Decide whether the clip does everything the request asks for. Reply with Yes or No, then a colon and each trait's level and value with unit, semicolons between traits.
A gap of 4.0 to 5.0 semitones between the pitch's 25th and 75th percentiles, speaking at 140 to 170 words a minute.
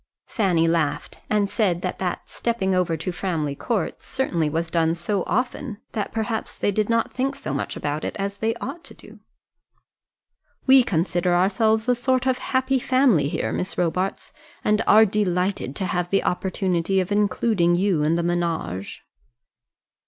Yes: average, 4.5 semitones; average, 165 wpm